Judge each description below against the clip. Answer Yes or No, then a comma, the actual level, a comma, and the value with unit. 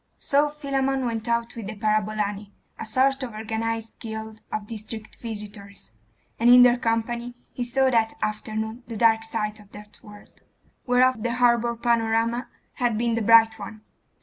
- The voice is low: No, high, 225 Hz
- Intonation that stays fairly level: Yes, narrow, 1.9 semitones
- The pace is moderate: Yes, average, 160 wpm